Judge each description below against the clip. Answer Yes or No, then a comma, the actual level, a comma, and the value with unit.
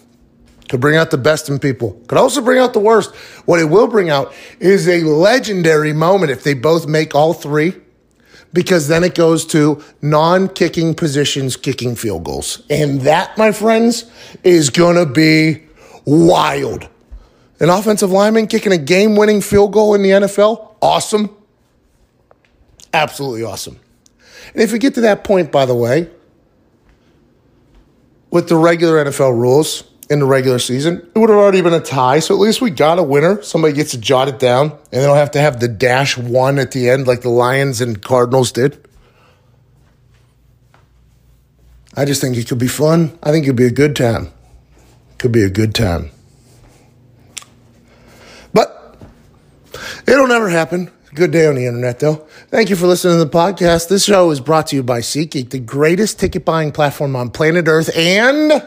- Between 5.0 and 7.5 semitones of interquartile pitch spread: Yes, wide, 5.6 semitones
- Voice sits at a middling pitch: Yes, medium, 155 Hz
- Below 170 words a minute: No, average, 175 wpm